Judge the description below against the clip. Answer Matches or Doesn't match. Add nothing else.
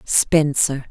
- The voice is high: Doesn't match